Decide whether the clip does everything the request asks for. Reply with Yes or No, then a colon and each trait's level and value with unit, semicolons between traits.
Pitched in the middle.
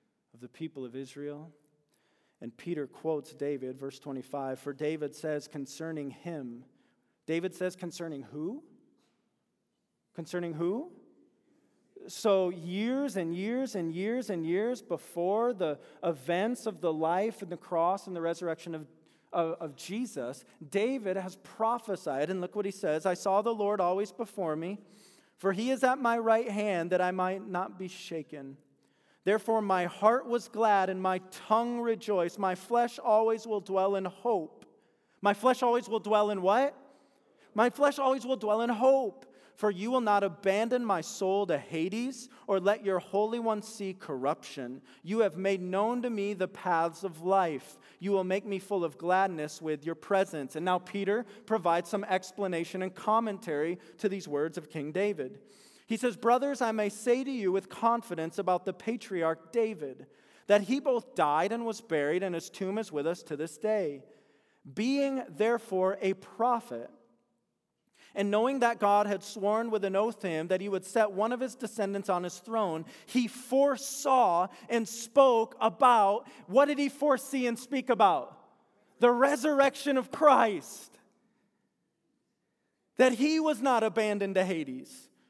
No: high, 195 Hz